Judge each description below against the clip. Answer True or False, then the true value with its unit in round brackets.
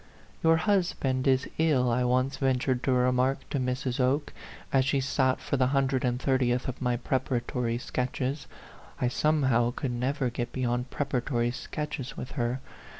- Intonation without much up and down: True (1.6 semitones)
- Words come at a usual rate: True (170 wpm)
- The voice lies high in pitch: False (130 Hz)